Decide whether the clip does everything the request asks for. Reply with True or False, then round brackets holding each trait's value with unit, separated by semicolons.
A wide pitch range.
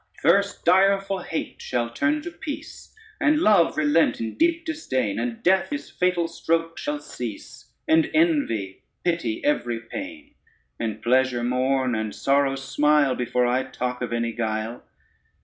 True (8.7 semitones)